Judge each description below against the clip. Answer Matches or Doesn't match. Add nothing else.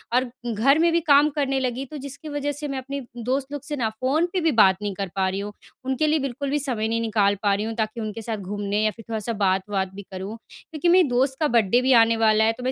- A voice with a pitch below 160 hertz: Doesn't match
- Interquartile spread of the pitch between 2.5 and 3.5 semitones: Doesn't match